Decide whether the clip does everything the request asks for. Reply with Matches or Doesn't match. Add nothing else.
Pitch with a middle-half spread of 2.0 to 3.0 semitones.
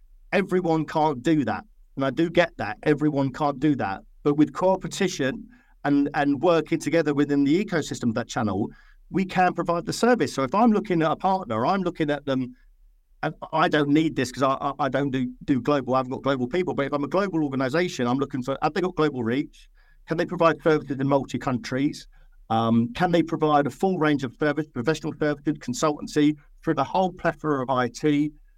Doesn't match